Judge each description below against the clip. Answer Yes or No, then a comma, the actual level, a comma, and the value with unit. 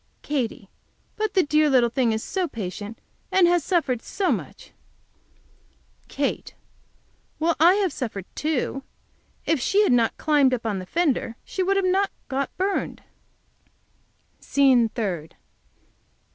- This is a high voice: Yes, very high, 280 Hz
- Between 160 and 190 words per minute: No, slow, 135 wpm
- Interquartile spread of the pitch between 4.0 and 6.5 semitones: No, wide, 7.4 semitones